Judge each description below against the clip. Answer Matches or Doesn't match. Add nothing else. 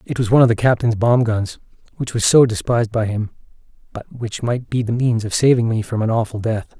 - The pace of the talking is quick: Matches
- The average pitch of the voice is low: Matches